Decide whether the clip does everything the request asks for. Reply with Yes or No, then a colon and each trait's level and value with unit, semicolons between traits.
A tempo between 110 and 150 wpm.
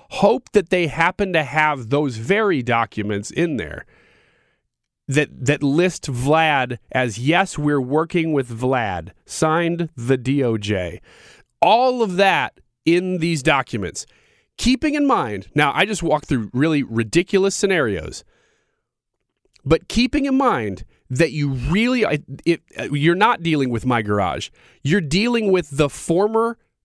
Yes: slow, 135 wpm